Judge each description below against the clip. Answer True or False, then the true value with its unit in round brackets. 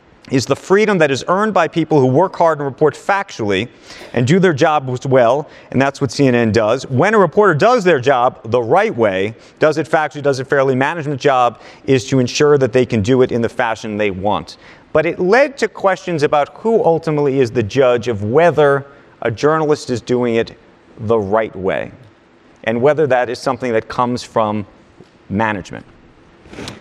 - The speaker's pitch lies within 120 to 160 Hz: True (135 Hz)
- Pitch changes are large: False (4.7 semitones)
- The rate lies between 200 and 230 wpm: False (190 wpm)